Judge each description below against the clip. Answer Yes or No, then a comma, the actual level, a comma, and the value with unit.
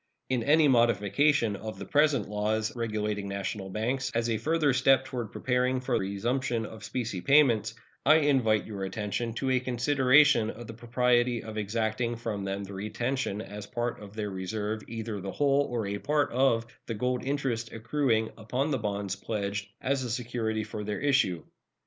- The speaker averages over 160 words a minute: Yes, average, 175 wpm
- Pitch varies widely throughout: No, average, 3.5 semitones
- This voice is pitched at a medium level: No, low, 115 Hz